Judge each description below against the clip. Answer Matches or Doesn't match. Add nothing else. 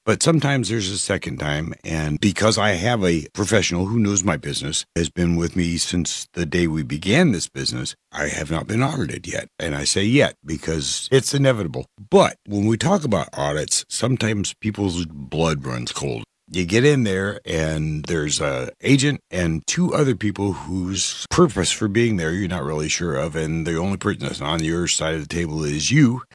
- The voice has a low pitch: Matches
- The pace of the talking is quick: Doesn't match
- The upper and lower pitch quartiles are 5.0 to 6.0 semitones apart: Matches